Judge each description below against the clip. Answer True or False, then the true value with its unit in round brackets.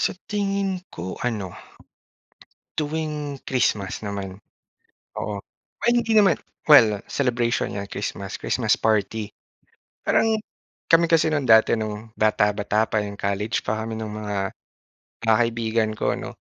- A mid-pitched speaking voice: False (110 Hz)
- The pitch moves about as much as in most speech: False (6.1 semitones)